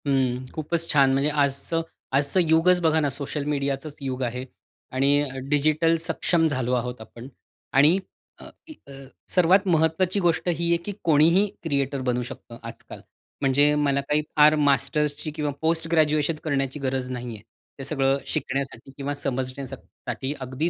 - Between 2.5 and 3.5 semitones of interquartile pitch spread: Yes, average, 3.0 semitones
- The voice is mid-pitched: Yes, medium, 145 Hz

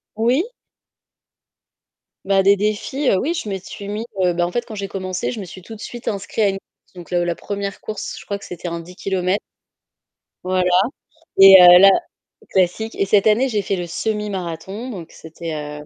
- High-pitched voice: Yes, high, 195 Hz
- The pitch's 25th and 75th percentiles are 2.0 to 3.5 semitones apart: Yes, average, 3.0 semitones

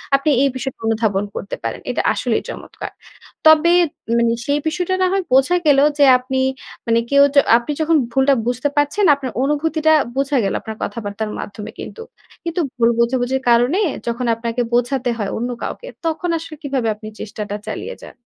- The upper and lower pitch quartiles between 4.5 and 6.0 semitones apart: Yes, average, 4.8 semitones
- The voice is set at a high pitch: Yes, very high, 265 Hz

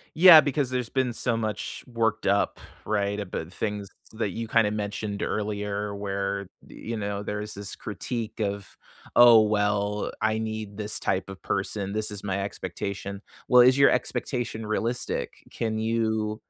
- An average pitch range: No, narrow, 2.1 semitones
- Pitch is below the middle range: Yes, low, 105 Hz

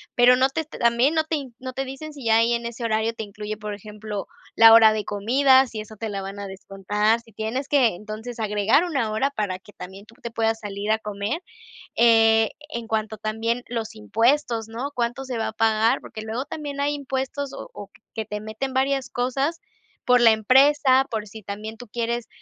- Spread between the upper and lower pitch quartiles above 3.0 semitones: Yes, average, 3.4 semitones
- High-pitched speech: Yes, high, 225 Hz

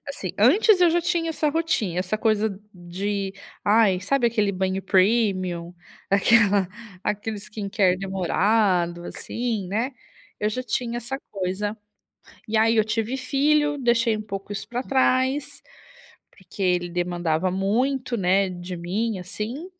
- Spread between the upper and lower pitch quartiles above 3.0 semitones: Yes, average, 4.5 semitones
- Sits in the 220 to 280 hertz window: No, high, 210 Hz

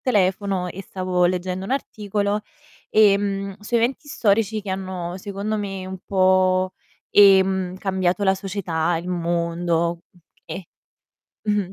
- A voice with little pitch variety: Yes, narrow, 1.9 semitones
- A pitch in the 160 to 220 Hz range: Yes, high, 190 Hz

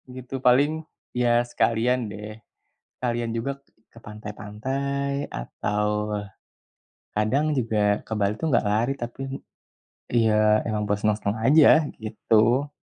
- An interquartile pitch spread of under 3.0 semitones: No, average, 3.7 semitones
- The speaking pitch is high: No, low, 115 Hz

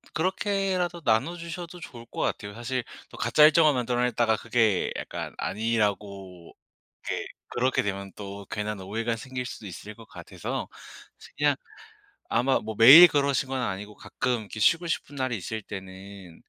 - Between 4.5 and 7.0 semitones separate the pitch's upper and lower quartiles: Yes, wide, 5.4 semitones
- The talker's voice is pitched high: No, low, 115 Hz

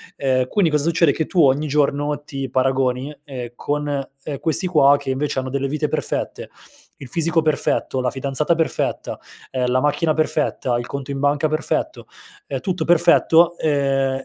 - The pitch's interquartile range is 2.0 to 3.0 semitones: Yes, narrow, 2.5 semitones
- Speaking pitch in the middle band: Yes, medium, 145 Hz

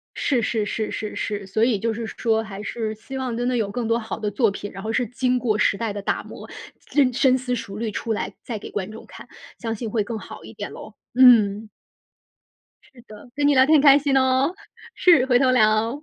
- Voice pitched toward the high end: Yes, high, 230 Hz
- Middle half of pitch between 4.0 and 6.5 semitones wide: No, average, 3.0 semitones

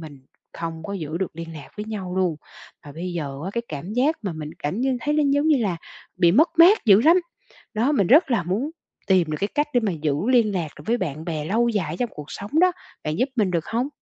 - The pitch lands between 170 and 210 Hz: Yes, high, 195 Hz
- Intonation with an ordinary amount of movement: No, wide, 7.0 semitones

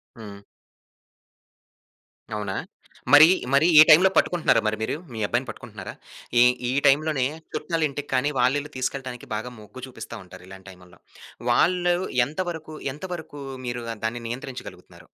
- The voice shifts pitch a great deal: Yes, wide, 5.9 semitones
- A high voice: No, low, 130 Hz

